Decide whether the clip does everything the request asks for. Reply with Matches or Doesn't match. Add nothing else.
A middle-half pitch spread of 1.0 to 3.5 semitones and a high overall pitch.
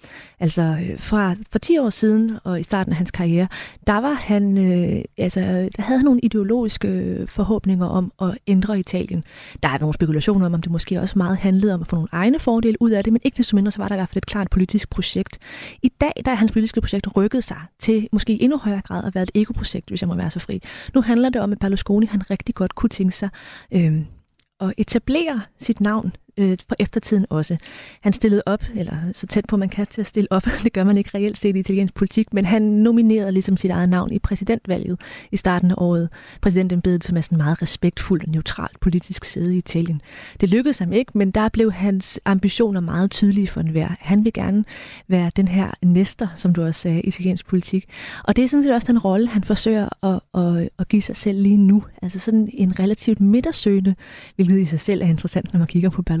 Matches